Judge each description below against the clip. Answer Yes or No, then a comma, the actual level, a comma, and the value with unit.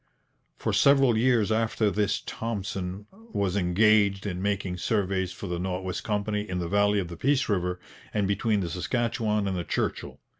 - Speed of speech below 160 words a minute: No, average, 175 wpm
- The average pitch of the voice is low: Yes, low, 100 Hz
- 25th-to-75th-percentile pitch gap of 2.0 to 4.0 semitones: Yes, average, 2.9 semitones